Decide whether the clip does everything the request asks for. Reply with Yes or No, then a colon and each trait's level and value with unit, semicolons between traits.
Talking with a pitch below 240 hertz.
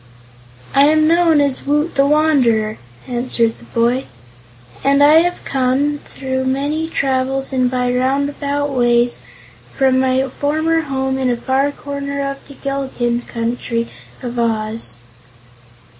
No: very high, 270 Hz